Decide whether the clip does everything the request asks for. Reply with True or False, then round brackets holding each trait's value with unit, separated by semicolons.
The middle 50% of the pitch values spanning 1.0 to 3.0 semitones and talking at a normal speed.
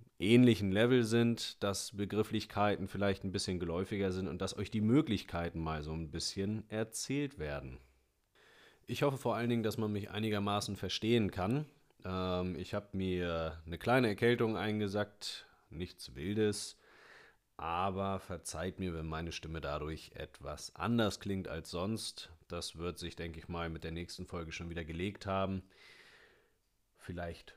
False (4.2 semitones; 150 wpm)